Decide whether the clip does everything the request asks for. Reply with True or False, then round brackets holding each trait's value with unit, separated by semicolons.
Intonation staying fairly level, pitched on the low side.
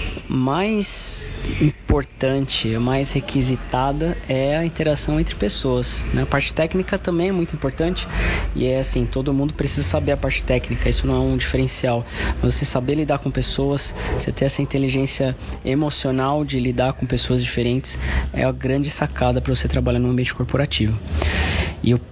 True (2.3 semitones; 130 Hz)